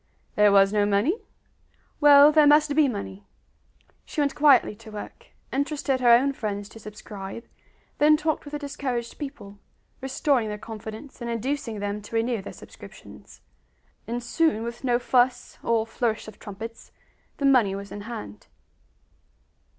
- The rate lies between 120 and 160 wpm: Yes, average, 150 wpm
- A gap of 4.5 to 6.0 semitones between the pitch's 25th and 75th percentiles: Yes, average, 5.1 semitones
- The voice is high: Yes, high, 235 Hz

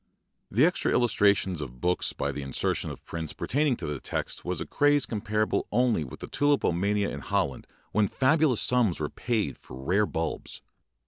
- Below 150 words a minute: No, average, 170 wpm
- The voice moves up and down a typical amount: No, wide, 7.5 semitones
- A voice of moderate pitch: No, low, 105 Hz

